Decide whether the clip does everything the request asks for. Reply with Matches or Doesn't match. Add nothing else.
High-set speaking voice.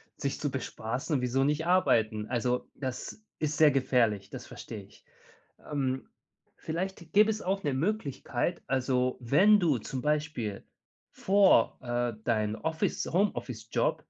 Doesn't match